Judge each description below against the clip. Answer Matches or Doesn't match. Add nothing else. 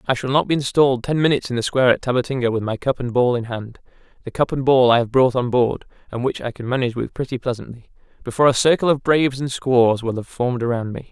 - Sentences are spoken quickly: Matches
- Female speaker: Doesn't match